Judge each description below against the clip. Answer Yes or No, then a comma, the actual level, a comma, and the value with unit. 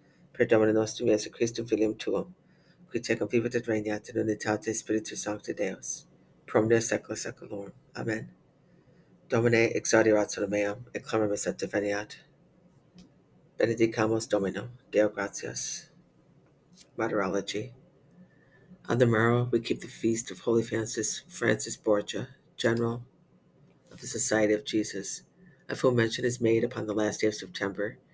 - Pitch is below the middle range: Yes, low, 115 Hz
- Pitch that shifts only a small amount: Yes, narrow, 2.3 semitones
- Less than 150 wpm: Yes, slow, 135 wpm